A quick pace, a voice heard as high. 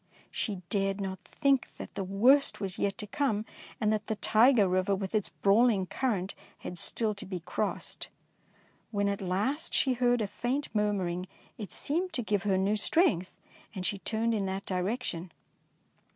No: average, 170 wpm; high, 205 Hz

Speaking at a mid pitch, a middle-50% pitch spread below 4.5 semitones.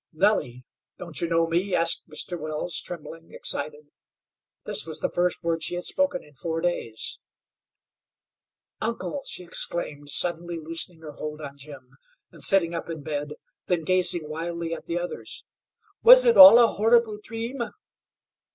Yes: medium, 170 Hz; average, 3.2 semitones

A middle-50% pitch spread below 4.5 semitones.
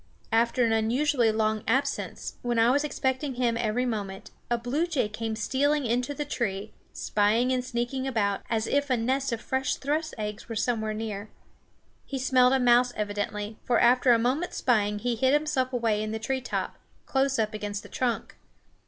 Yes: average, 3.3 semitones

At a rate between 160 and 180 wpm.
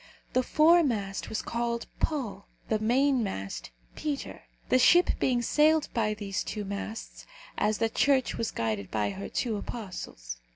No: average, 140 wpm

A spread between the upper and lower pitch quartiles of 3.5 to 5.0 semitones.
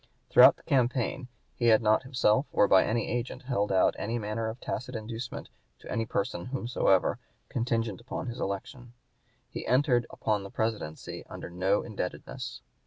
No: average, 2.9 semitones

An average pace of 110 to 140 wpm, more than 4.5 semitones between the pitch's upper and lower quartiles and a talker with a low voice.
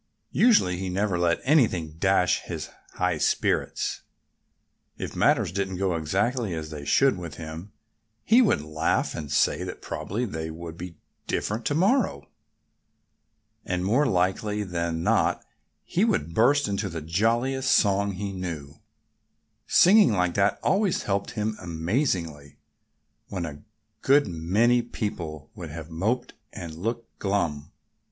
Yes: slow, 135 wpm; wide, 5.6 semitones; very low, 95 Hz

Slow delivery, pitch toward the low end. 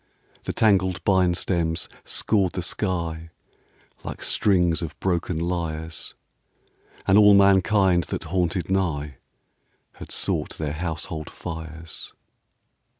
Yes: slow, 105 wpm; very low, 85 Hz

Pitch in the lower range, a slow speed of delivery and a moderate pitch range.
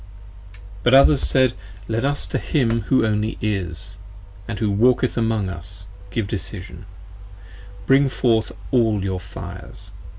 Yes: low, 110 Hz; slow, 130 wpm; average, 4.0 semitones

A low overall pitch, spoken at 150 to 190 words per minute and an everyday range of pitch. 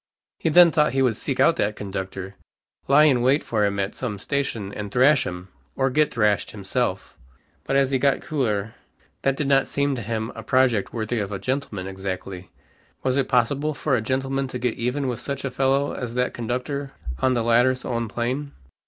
No: low, 125 Hz; average, 200 wpm; average, 4.3 semitones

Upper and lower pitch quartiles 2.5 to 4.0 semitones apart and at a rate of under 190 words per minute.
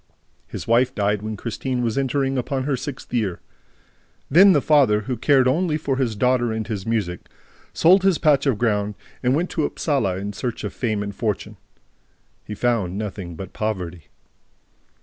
No: average, 4.7 semitones; average, 170 wpm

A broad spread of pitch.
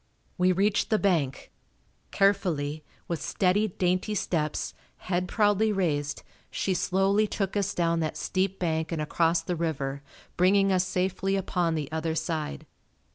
No: average, 3.4 semitones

